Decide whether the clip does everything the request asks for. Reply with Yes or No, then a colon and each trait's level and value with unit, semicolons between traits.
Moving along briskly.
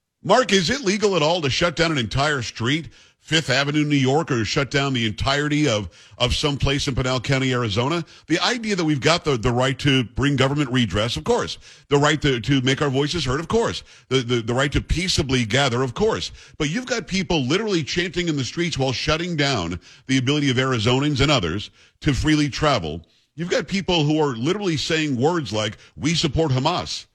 Yes: fast, 210 wpm